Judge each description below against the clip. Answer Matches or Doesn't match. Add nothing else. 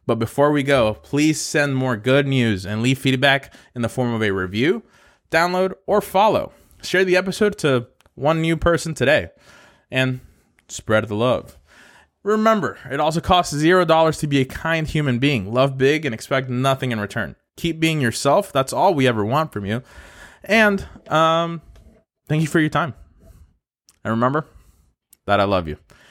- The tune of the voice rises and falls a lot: Matches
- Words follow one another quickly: Doesn't match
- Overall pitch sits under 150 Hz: Matches